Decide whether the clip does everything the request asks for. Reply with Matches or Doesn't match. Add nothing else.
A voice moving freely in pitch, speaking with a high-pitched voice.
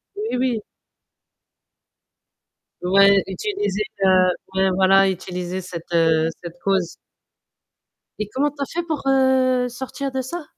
Matches